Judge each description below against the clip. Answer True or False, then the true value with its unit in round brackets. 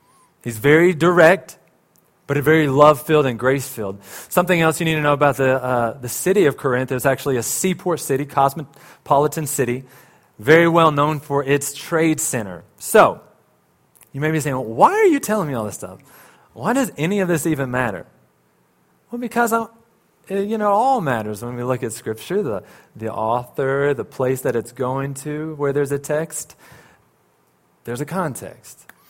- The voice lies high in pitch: False (140 Hz)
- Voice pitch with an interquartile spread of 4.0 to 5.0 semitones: True (4.6 semitones)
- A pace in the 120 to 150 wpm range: False (175 wpm)